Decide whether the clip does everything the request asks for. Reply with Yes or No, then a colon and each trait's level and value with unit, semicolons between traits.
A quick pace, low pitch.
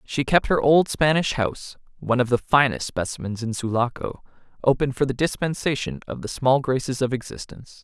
No: average, 175 wpm; low, 130 Hz